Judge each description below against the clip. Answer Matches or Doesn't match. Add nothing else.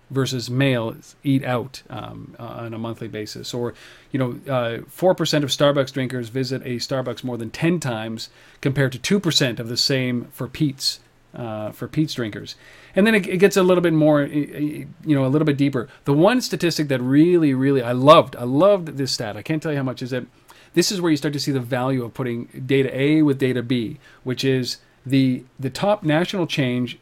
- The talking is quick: Matches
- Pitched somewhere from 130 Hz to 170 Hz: Matches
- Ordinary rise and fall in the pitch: Matches